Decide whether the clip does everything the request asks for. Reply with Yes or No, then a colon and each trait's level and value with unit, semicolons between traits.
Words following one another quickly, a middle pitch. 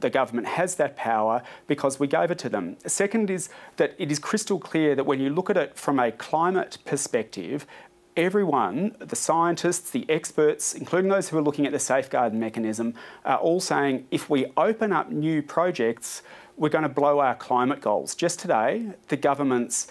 No: average, 185 wpm; medium, 155 Hz